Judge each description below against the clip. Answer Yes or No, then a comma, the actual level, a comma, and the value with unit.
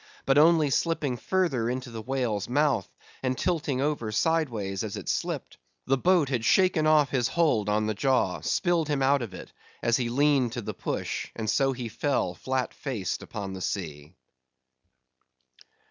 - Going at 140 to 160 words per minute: No, average, 170 wpm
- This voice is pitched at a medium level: No, low, 130 Hz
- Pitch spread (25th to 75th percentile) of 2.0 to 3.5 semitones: No, average, 5.0 semitones